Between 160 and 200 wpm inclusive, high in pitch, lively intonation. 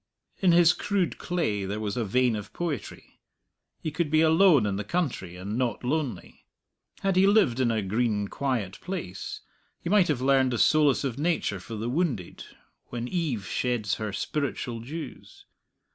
No: average, 170 wpm; low, 125 Hz; wide, 7.2 semitones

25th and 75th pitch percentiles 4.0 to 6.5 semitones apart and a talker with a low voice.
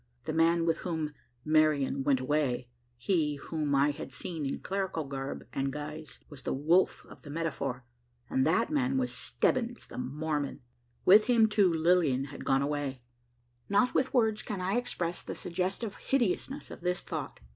No: wide, 5.4 semitones; medium, 160 Hz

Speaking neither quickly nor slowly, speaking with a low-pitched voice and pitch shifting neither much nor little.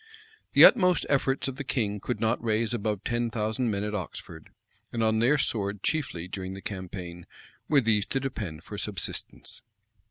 Yes: average, 170 wpm; low, 110 Hz; average, 4.2 semitones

